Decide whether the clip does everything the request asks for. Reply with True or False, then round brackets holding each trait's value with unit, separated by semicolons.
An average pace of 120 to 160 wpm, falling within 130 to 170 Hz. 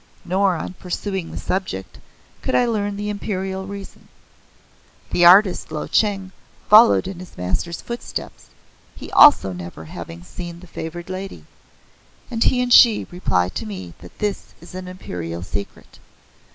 False (150 wpm; 185 Hz)